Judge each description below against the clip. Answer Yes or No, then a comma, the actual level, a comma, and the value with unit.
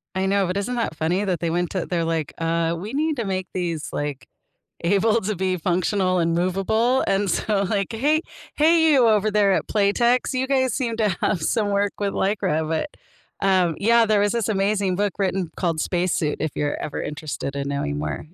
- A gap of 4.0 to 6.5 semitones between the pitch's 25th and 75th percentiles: Yes, average, 4.3 semitones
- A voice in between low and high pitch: No, high, 195 Hz